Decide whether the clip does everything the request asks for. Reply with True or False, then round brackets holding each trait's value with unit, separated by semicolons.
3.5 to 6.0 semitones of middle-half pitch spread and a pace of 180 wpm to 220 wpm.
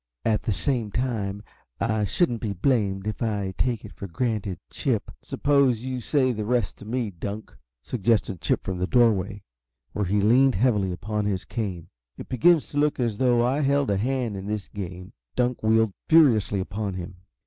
True (4.1 semitones; 185 wpm)